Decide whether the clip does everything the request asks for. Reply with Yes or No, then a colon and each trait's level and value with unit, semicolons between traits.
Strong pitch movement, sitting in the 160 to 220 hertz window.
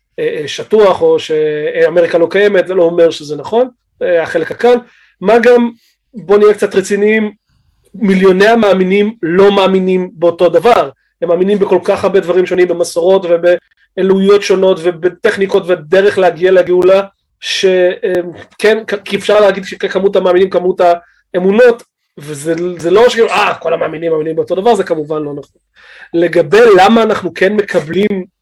No: average, 3.2 semitones; high, 190 Hz